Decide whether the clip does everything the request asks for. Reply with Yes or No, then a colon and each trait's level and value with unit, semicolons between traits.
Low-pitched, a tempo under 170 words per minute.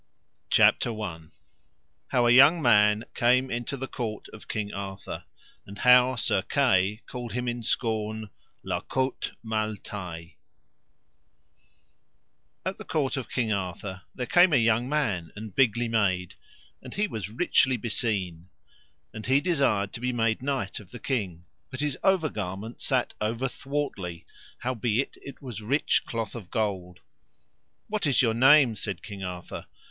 Yes: low, 115 Hz; average, 150 wpm